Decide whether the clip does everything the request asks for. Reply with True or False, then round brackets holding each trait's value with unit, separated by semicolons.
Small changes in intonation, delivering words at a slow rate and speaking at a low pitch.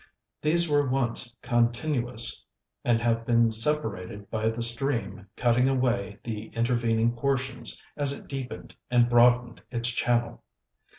True (1.8 semitones; 125 wpm; 120 Hz)